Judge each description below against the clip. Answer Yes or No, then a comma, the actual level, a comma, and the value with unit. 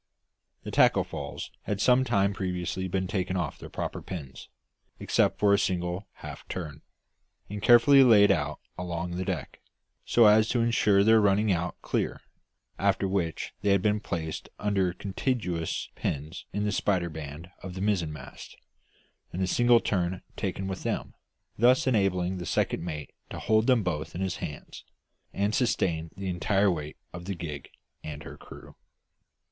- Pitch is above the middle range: No, very low, 95 Hz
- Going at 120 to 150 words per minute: No, average, 165 wpm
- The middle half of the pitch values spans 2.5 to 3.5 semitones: Yes, average, 3.2 semitones